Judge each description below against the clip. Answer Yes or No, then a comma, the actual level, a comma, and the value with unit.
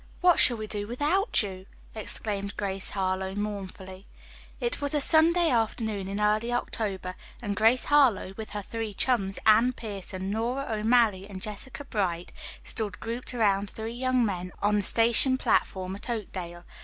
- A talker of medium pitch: No, high, 215 Hz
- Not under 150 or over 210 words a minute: Yes, average, 155 wpm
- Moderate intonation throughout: Yes, average, 3.8 semitones